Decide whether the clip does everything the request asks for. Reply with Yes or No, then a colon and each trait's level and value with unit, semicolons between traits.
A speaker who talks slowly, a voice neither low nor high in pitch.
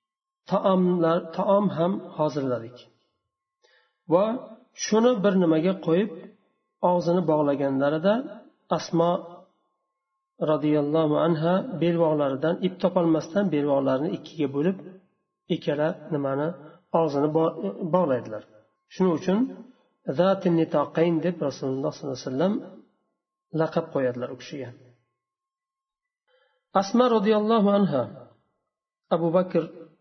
Yes: slow, 85 wpm; medium, 175 Hz